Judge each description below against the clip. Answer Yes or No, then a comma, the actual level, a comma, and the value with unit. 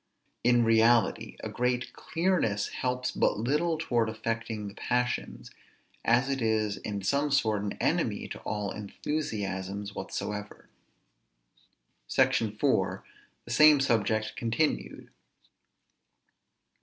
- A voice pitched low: Yes, low, 115 Hz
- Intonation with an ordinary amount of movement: Yes, average, 3.9 semitones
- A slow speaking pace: Yes, slow, 105 wpm